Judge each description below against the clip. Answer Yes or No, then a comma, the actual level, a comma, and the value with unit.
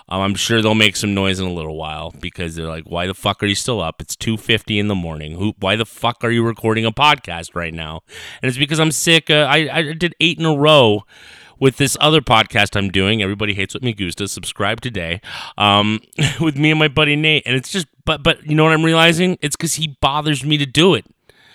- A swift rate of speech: Yes, fast, 240 wpm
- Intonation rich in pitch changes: Yes, wide, 7.8 semitones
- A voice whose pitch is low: Yes, low, 115 Hz